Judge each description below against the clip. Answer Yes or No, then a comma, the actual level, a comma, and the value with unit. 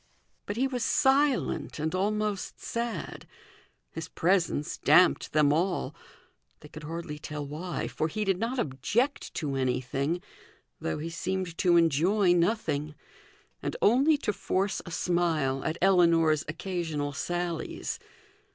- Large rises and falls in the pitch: No, average, 4.6 semitones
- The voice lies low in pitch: No, medium, 175 Hz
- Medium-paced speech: No, slow, 130 wpm